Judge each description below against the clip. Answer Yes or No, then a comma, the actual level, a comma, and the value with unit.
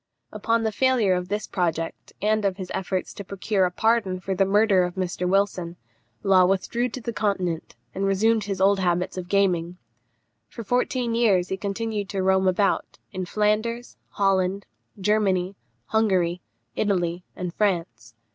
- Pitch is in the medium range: No, high, 195 Hz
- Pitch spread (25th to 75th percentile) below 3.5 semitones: Yes, average, 2.7 semitones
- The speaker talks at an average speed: Yes, average, 155 wpm